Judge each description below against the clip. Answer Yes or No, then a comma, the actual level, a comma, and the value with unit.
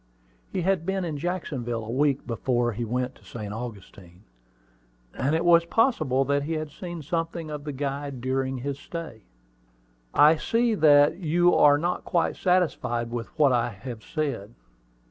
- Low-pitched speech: No, medium, 145 Hz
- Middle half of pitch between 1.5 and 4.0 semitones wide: No, wide, 5.5 semitones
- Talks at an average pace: Yes, average, 165 wpm